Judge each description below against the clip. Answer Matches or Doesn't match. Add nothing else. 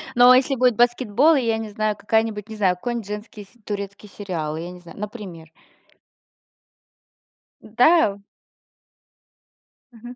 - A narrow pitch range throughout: Doesn't match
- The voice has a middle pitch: Doesn't match